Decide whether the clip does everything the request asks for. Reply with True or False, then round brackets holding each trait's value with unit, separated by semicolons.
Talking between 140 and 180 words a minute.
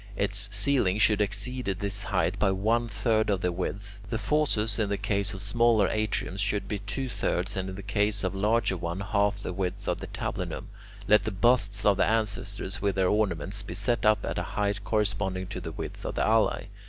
False (205 wpm)